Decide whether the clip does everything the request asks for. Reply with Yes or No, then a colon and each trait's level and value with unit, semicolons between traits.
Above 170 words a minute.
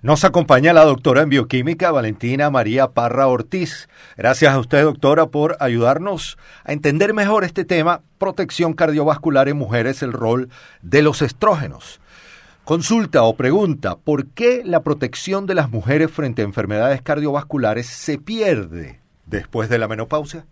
No: average, 145 wpm